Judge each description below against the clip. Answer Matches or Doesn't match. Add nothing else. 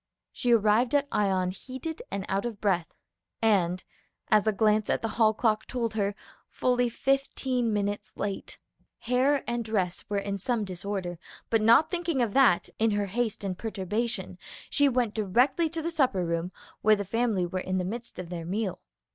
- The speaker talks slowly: Doesn't match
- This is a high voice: Matches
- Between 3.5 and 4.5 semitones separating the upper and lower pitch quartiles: Matches